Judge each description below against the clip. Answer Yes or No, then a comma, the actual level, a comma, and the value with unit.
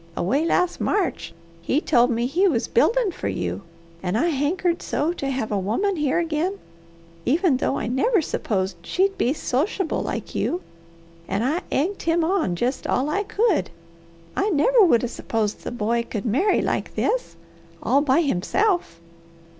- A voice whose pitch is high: Yes, very high, 300 Hz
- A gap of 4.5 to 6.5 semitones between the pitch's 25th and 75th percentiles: No, wide, 7.5 semitones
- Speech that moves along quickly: No, average, 165 wpm